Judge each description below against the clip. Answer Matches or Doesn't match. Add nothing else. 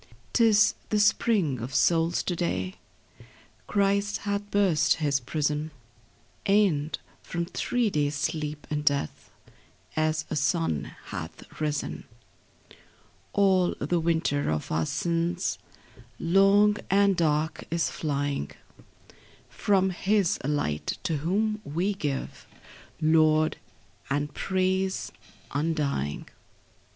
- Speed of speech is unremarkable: Doesn't match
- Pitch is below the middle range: Doesn't match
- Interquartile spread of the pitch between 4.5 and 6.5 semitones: Matches